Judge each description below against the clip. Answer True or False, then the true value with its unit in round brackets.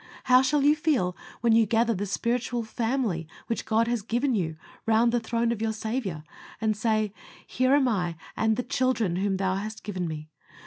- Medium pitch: False (225 Hz)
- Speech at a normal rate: True (190 wpm)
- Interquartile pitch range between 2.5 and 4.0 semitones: True (3.4 semitones)